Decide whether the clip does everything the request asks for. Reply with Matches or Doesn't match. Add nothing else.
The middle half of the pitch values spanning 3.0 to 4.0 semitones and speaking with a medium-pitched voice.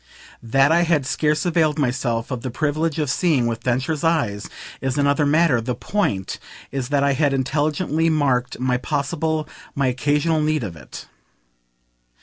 Matches